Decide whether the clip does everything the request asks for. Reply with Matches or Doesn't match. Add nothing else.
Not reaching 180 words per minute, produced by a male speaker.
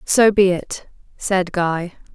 Doesn't match